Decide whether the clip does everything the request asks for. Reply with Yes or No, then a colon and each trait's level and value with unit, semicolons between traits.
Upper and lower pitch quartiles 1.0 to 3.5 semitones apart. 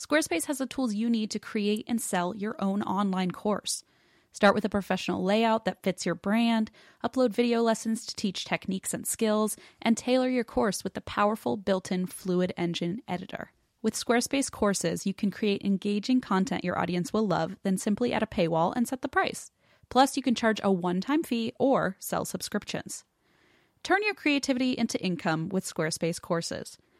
No: average, 4.4 semitones